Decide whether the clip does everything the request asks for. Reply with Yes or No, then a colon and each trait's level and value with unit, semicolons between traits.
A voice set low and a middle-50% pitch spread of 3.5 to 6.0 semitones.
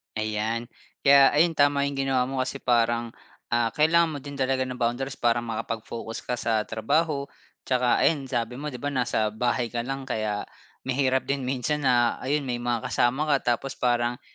No: low, 125 Hz; average, 2.8 semitones